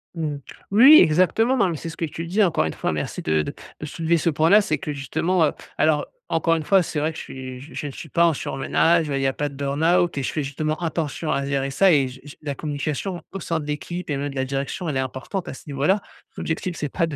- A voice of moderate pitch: Yes, medium, 155 Hz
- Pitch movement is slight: No, average, 3.5 semitones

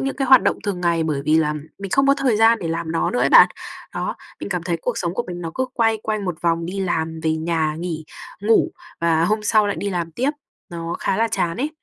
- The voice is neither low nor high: Yes, medium, 180 Hz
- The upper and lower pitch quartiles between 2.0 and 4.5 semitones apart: No, average, 5.1 semitones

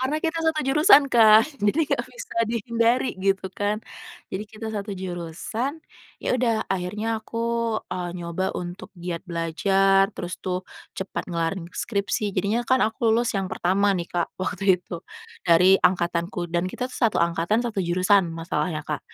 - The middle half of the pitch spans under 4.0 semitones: No, average, 4.4 semitones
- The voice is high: Yes, high, 195 Hz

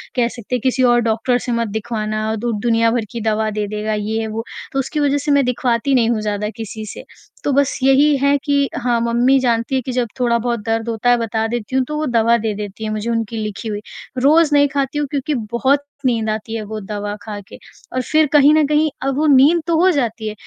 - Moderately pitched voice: No, high, 235 Hz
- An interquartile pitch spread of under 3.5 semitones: No, average, 3.8 semitones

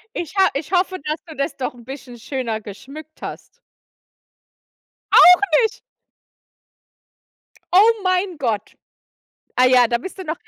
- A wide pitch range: Yes, wide, 6.3 semitones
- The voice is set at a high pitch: Yes, very high, 300 Hz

